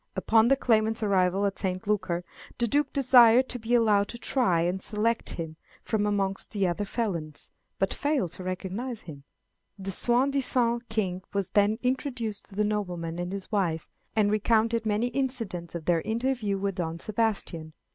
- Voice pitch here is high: Yes, high, 210 Hz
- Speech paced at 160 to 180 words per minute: Yes, average, 170 wpm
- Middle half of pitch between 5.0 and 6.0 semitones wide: No, average, 4.1 semitones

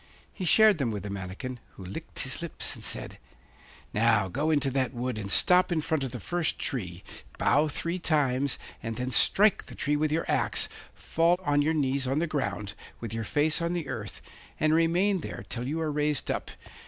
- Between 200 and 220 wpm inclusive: Yes, fast, 205 wpm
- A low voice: No, medium, 145 Hz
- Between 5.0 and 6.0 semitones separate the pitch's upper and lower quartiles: Yes, average, 5.3 semitones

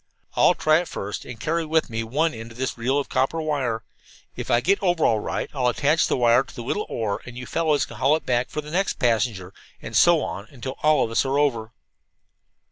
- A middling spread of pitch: Yes, average, 4.9 semitones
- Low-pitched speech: Yes, low, 130 Hz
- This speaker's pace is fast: Yes, fast, 235 wpm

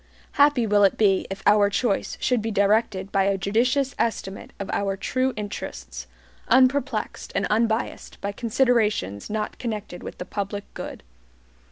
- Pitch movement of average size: Yes, average, 3.1 semitones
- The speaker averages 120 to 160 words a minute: Yes, average, 150 wpm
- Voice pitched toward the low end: No, high, 210 Hz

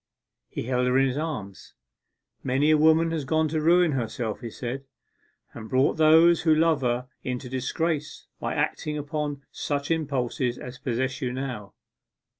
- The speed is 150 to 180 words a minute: Yes, average, 160 wpm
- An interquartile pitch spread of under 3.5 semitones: No, average, 3.8 semitones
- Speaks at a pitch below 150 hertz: Yes, low, 135 Hz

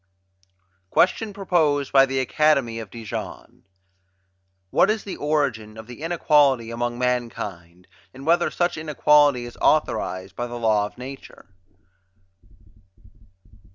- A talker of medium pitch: No, low, 130 Hz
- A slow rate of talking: Yes, slow, 120 wpm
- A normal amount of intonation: Yes, average, 4.9 semitones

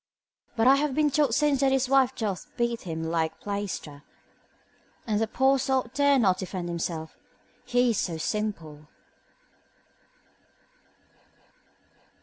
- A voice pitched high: Yes, high, 225 Hz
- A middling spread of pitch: No, wide, 7.4 semitones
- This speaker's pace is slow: Yes, slow, 130 wpm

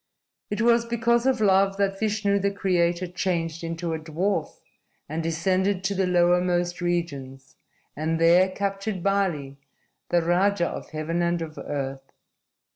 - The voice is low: No, medium, 175 Hz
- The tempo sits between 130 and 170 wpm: Yes, average, 140 wpm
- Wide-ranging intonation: No, average, 3.1 semitones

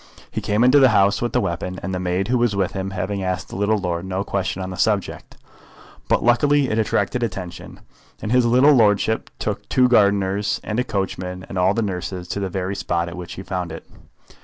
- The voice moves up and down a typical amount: Yes, average, 3.3 semitones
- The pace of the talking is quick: Yes, fast, 215 wpm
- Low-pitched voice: Yes, low, 100 Hz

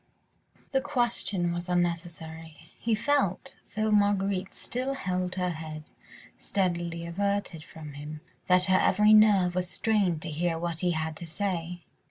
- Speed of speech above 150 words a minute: No, average, 145 wpm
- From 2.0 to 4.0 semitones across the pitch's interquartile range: Yes, average, 3.5 semitones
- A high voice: No, medium, 180 Hz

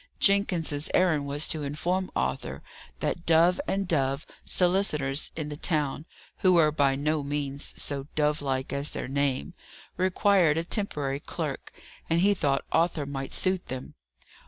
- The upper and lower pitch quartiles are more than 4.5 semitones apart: No, average, 3.8 semitones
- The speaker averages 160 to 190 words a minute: No, average, 150 wpm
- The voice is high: No, medium, 150 Hz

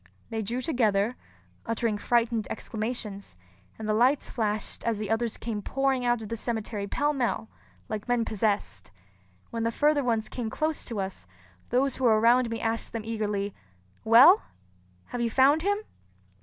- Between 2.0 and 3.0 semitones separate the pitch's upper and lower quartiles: Yes, narrow, 2.5 semitones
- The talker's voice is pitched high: Yes, high, 230 Hz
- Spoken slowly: No, average, 165 wpm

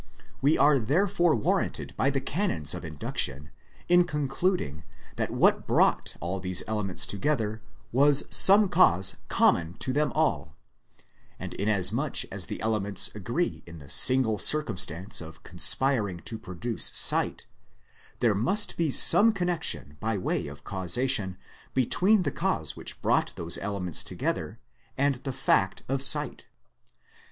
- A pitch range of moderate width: No, wide, 8.1 semitones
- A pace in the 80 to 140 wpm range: Yes, slow, 135 wpm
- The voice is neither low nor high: No, low, 115 Hz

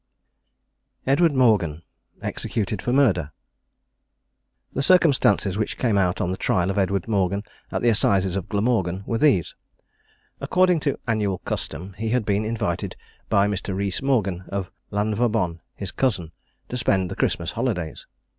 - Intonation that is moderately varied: Yes, average, 4.3 semitones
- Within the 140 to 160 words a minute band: Yes, average, 145 wpm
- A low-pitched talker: Yes, low, 100 Hz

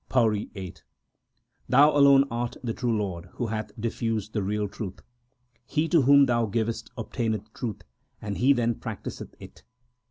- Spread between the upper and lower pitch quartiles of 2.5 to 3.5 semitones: Yes, average, 2.9 semitones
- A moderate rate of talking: Yes, average, 155 wpm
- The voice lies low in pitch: Yes, low, 115 Hz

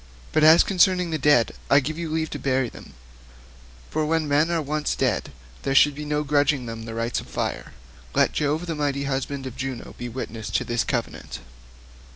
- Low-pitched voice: No, medium, 145 Hz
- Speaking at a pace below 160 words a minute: No, average, 195 wpm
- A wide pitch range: No, average, 3.0 semitones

